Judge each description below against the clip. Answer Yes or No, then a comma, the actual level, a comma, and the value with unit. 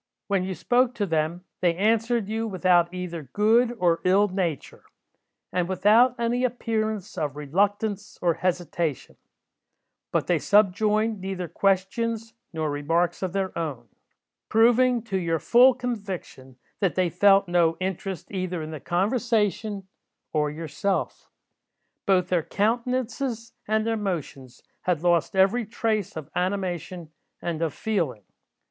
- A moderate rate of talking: No, slow, 130 wpm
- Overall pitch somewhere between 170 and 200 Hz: Yes, high, 190 Hz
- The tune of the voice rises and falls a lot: No, average, 4.3 semitones